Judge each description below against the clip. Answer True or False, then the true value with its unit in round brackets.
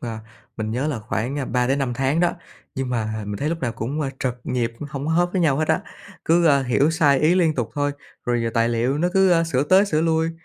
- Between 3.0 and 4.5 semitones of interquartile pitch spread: False (4.9 semitones)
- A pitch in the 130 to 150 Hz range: True (140 Hz)